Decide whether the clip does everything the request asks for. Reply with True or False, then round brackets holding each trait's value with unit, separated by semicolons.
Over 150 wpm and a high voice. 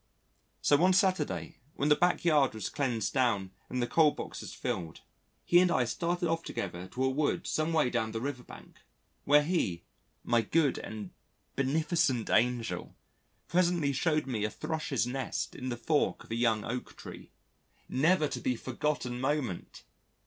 False (165 wpm; 135 Hz)